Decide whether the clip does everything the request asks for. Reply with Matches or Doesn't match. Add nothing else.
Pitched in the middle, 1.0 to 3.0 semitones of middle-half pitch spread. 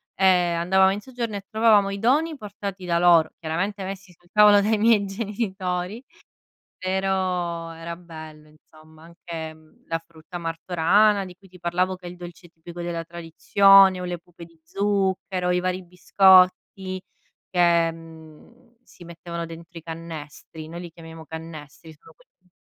Matches